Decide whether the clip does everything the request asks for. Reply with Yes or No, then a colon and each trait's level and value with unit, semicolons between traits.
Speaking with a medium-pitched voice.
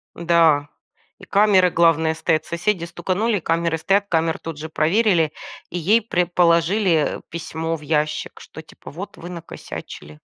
Yes: medium, 170 Hz